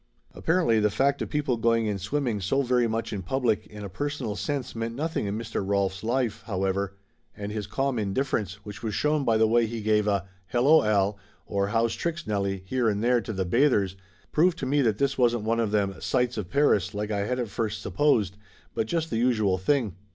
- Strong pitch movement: No, average, 4.1 semitones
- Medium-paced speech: No, fast, 215 wpm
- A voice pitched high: No, low, 110 Hz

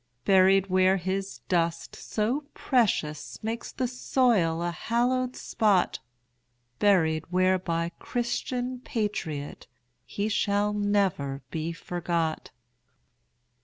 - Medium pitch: No, high, 195 Hz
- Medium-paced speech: No, slow, 95 wpm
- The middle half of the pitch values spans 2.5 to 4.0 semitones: No, average, 4.9 semitones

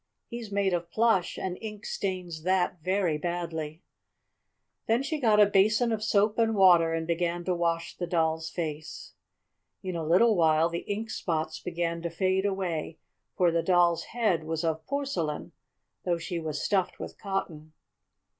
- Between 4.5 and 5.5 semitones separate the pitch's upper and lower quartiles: No, average, 3.5 semitones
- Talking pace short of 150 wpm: No, average, 165 wpm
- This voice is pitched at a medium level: Yes, medium, 175 Hz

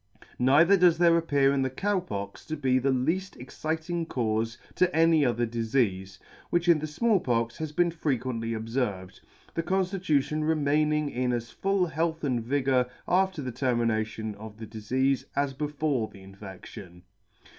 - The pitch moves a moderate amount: No, wide, 5.8 semitones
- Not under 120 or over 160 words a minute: Yes, average, 155 wpm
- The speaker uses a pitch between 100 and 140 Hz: Yes, low, 135 Hz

